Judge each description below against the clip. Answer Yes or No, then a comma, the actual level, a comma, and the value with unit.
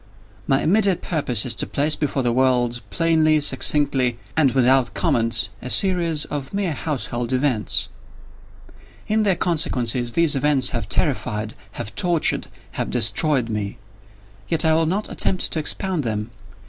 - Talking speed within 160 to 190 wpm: No, slow, 135 wpm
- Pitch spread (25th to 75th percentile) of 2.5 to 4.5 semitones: No, average, 5.1 semitones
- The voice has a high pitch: No, medium, 140 Hz